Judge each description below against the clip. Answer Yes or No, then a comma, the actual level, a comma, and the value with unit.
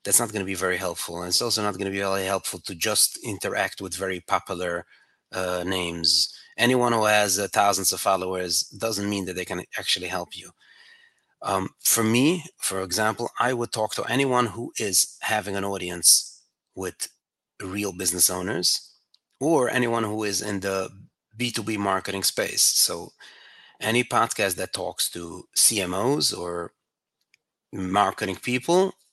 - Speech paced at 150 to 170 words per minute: Yes, average, 160 wpm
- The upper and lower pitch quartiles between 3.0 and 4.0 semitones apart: Yes, average, 3.5 semitones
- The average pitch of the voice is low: Yes, low, 100 Hz